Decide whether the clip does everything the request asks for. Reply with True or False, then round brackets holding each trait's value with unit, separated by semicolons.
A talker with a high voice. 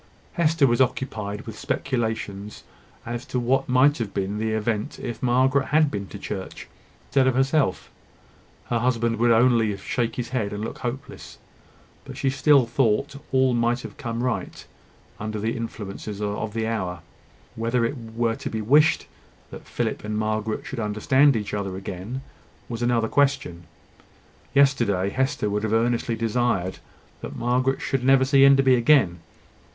False (115 Hz)